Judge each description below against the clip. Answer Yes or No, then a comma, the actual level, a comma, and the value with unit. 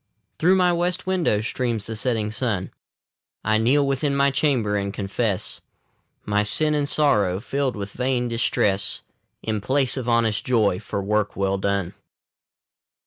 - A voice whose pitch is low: Yes, low, 115 Hz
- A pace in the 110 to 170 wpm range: Yes, average, 145 wpm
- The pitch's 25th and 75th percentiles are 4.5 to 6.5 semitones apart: Yes, average, 5.1 semitones